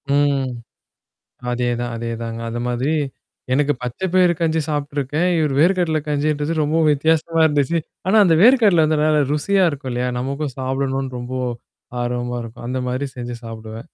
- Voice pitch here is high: No, medium, 140 Hz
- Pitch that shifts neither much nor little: Yes, average, 4.4 semitones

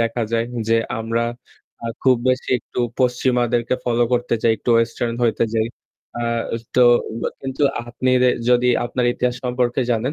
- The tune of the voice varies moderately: No, narrow, 1.3 semitones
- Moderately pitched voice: No, low, 120 Hz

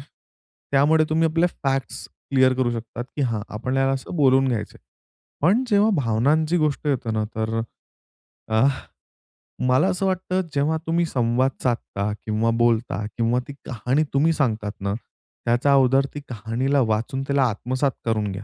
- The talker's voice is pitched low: Yes, low, 130 Hz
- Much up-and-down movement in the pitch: No, average, 4.2 semitones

